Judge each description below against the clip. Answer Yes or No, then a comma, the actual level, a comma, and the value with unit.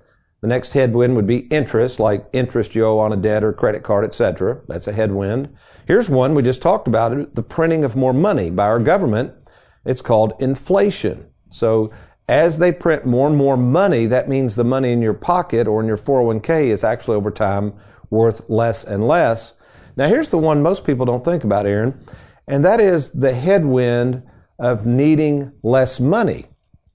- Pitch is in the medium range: No, low, 125 Hz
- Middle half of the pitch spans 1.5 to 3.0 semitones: No, average, 4.1 semitones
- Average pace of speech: Yes, average, 185 wpm